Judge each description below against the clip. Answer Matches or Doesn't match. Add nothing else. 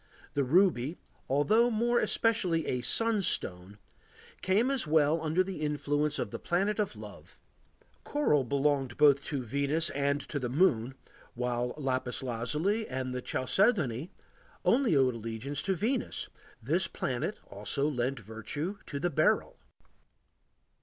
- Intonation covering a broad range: Matches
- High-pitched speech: Doesn't match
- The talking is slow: Matches